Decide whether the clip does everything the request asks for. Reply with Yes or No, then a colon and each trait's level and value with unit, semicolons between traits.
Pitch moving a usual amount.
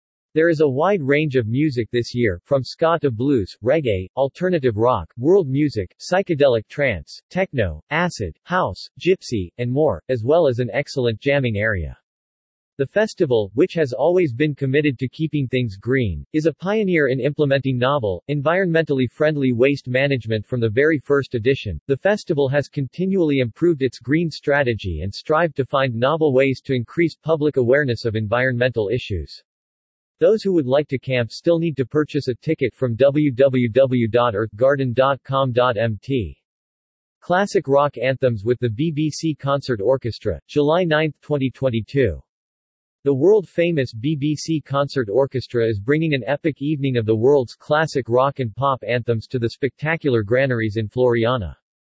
Yes: average, 4.2 semitones